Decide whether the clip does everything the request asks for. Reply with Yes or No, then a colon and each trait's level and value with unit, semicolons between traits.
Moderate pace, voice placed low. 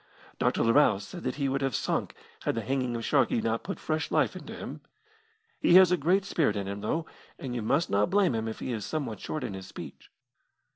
No: fast, 230 wpm; low, 125 Hz